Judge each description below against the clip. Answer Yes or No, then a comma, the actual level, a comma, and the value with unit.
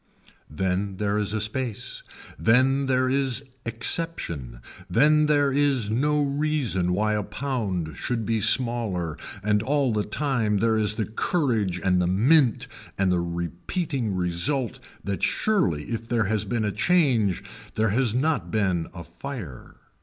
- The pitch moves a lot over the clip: Yes, wide, 5.8 semitones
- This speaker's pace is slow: No, average, 145 wpm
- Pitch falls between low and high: No, low, 110 Hz